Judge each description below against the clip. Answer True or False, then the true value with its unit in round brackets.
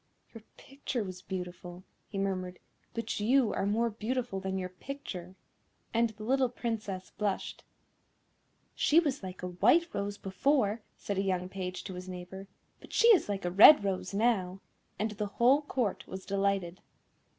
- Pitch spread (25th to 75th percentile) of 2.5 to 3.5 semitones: False (4.0 semitones)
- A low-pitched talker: False (200 Hz)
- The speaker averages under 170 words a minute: True (160 wpm)